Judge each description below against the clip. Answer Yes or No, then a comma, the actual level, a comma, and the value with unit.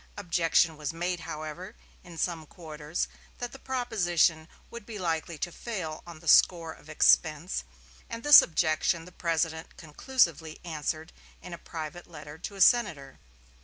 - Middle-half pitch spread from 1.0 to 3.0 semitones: Yes, narrow, 2.5 semitones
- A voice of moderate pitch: Yes, medium, 165 Hz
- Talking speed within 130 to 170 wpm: Yes, average, 150 wpm